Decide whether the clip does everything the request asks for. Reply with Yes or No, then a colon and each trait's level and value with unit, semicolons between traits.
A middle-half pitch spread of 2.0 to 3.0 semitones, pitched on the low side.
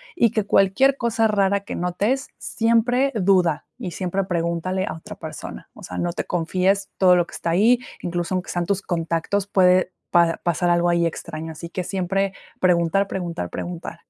No: narrow, 2.6 semitones; medium, 185 Hz